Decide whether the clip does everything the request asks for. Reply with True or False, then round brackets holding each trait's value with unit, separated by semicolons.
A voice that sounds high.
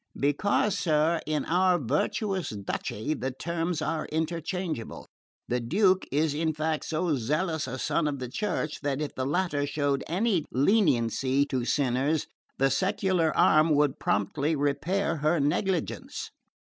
False (155 Hz)